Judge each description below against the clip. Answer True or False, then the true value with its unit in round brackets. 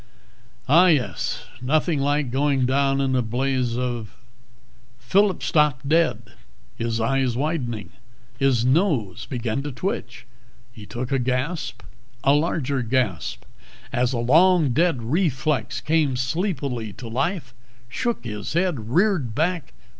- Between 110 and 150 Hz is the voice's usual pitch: True (135 Hz)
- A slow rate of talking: True (130 wpm)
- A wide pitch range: False (4.4 semitones)